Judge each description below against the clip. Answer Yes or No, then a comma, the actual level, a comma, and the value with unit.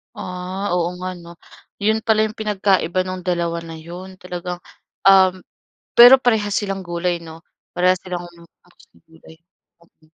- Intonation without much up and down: Yes, narrow, 2.1 semitones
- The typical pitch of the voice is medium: Yes, medium, 180 Hz